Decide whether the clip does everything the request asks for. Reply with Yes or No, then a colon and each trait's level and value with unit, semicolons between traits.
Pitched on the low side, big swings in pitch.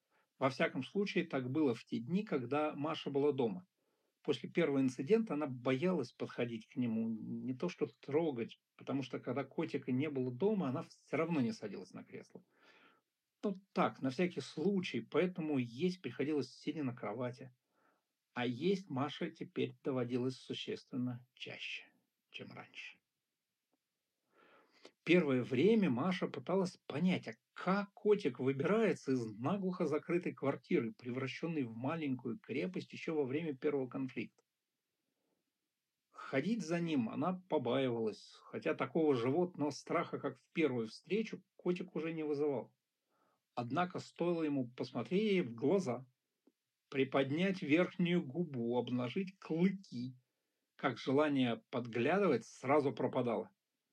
No: medium, 145 Hz; wide, 5.8 semitones